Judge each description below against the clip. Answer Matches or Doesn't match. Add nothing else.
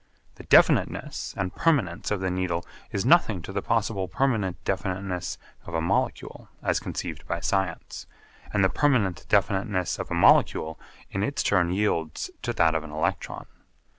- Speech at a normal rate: Matches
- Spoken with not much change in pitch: Doesn't match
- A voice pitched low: Matches